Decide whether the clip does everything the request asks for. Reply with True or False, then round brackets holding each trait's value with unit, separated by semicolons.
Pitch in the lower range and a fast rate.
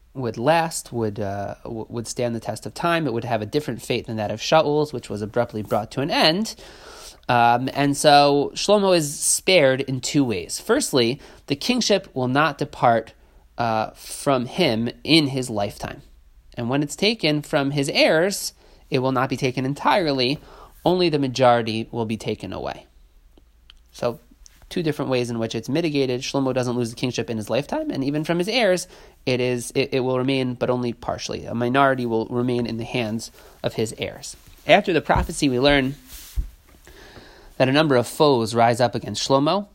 False (125 Hz; 185 wpm)